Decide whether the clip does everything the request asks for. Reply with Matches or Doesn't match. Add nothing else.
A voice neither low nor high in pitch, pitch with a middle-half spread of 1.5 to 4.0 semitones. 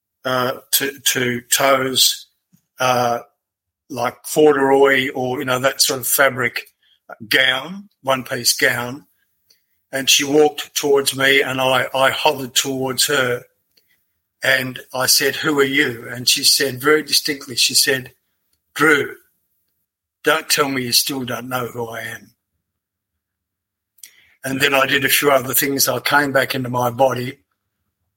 Doesn't match